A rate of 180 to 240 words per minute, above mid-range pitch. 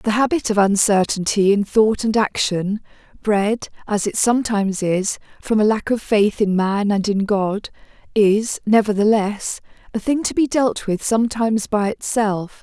No: average, 160 wpm; high, 210 Hz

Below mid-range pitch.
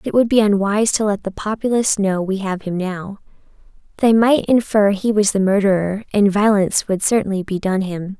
No: high, 200 Hz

